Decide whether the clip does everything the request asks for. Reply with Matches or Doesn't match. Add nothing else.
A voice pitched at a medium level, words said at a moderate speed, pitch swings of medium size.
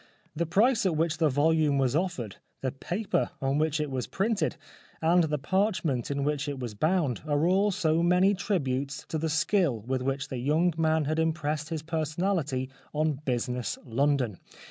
Matches